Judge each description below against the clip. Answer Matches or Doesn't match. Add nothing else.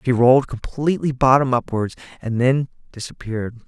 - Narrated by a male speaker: Matches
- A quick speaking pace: Doesn't match